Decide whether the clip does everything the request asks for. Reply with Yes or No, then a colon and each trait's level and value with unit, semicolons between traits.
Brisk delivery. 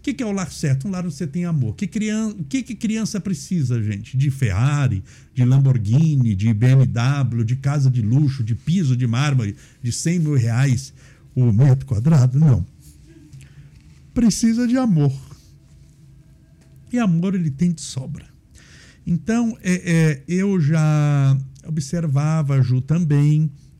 No: average, 150 wpm